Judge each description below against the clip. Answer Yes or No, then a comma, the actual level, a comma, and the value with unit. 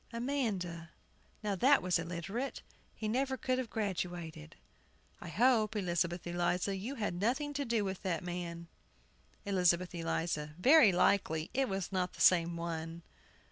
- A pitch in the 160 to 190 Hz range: Yes, medium, 185 Hz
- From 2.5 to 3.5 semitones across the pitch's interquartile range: No, average, 5.1 semitones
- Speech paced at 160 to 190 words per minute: No, average, 140 wpm